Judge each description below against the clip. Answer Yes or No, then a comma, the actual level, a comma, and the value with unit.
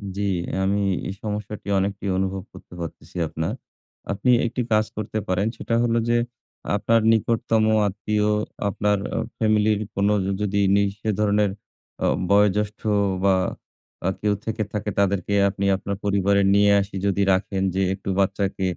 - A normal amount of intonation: No, narrow, 1.5 semitones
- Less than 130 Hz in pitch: Yes, low, 100 Hz